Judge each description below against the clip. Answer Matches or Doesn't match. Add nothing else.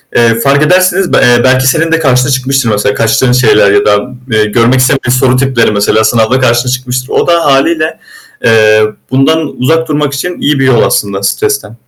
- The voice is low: Matches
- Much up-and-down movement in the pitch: Doesn't match